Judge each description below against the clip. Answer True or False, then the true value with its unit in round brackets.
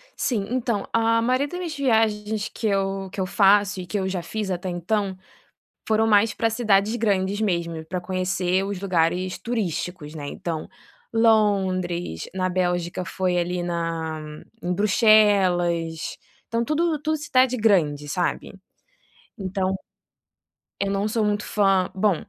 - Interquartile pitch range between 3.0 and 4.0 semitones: True (3.5 semitones)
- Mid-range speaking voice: False (195 Hz)